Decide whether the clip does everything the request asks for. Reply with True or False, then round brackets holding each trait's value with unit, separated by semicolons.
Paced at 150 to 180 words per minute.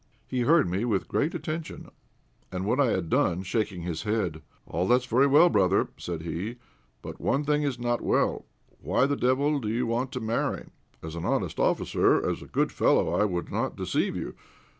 False (195 wpm)